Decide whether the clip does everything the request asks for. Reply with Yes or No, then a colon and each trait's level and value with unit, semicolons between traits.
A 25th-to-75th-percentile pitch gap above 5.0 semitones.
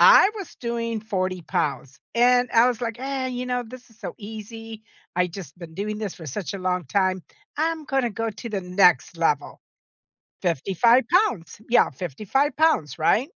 Yes: wide, 5.4 semitones